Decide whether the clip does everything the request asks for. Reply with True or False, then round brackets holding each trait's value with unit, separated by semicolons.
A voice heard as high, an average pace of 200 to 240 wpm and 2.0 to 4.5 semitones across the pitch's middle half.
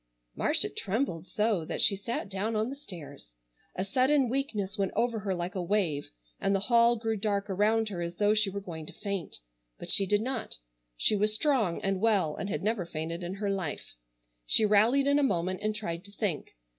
True (200 Hz; 205 wpm; 3.3 semitones)